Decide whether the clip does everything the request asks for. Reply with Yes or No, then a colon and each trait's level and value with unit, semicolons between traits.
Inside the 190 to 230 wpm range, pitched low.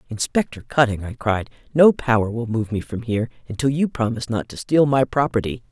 Yes: average, 200 wpm; low, 120 Hz